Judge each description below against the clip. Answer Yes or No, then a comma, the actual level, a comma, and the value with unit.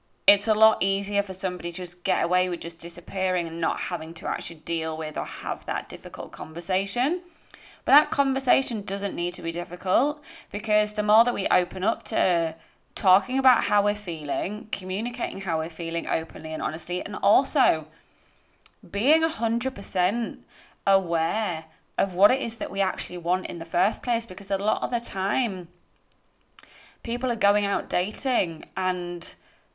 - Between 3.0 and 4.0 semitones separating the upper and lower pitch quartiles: No, average, 4.8 semitones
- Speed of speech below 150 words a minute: No, average, 170 wpm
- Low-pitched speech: No, high, 195 Hz